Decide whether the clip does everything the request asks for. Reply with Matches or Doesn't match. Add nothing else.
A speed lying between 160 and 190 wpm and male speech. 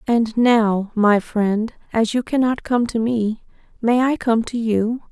Doesn't match